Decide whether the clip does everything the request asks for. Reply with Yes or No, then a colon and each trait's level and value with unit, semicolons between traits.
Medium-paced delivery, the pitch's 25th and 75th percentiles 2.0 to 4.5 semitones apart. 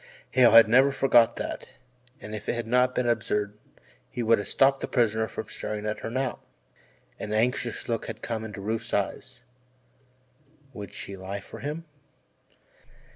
Yes: average, 165 wpm; average, 2.8 semitones